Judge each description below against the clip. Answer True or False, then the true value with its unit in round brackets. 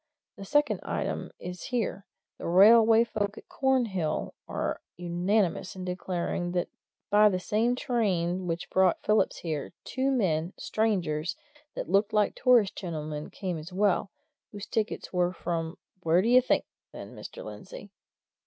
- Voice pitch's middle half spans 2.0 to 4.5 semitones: True (4.1 semitones)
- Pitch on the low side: False (190 Hz)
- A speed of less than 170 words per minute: True (145 wpm)